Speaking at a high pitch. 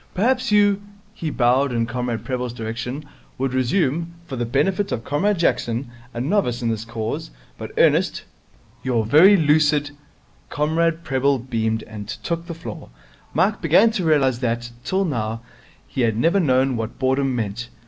No: low, 130 Hz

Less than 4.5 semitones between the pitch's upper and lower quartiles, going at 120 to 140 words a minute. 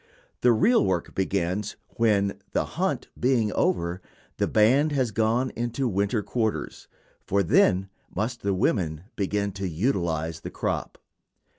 Yes: average, 4.0 semitones; slow, 135 wpm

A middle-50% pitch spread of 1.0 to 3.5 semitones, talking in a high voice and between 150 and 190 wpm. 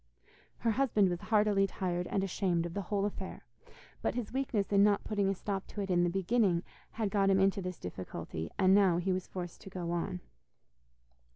No: narrow, 2.5 semitones; high, 195 Hz; average, 200 wpm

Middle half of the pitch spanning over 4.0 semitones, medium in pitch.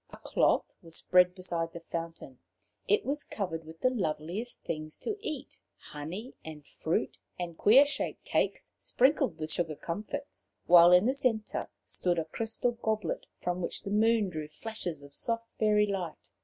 Yes: wide, 5.6 semitones; medium, 180 Hz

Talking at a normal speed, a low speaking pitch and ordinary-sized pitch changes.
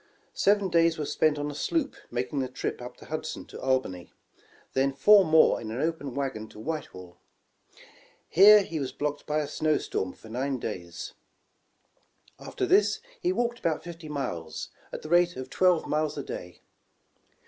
No: average, 175 wpm; medium, 150 Hz; average, 4.7 semitones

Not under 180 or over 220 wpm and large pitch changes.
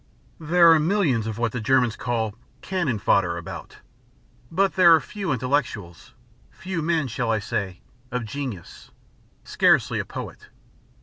No: average, 140 wpm; wide, 6.9 semitones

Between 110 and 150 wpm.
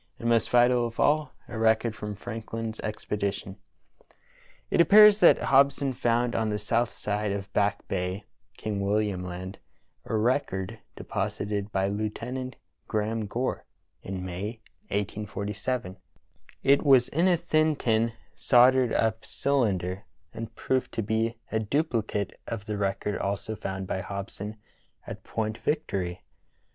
Yes: average, 140 wpm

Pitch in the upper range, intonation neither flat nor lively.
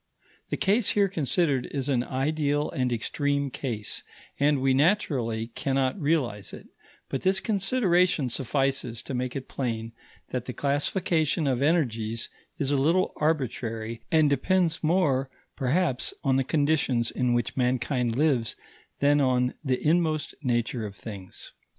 No: low, 135 Hz; average, 4.1 semitones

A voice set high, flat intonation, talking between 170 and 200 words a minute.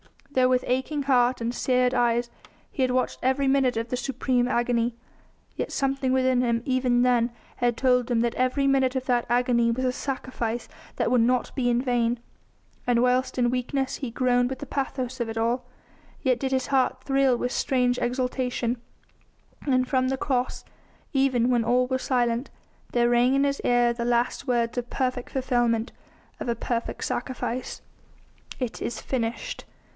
Yes: very high, 250 Hz; narrow, 1.4 semitones; average, 175 wpm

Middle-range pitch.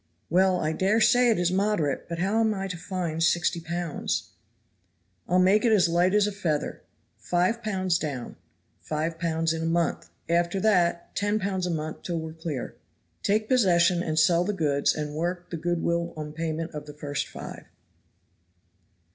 Yes: medium, 170 Hz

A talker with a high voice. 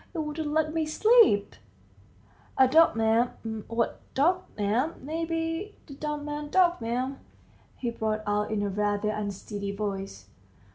Yes: very high, 255 Hz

